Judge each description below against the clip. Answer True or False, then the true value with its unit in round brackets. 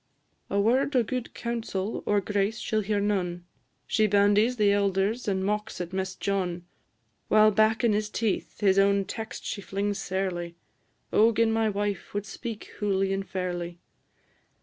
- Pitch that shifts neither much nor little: False (2.1 semitones)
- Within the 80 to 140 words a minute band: False (165 wpm)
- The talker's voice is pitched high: True (205 Hz)